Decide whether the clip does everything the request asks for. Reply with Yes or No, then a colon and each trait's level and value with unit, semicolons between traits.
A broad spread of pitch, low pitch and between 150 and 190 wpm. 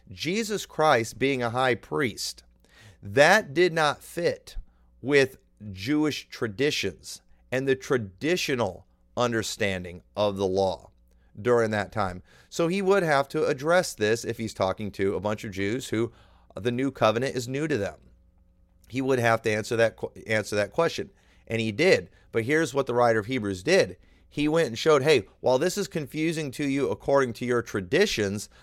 Yes: wide, 6.2 semitones; low, 115 Hz; average, 170 wpm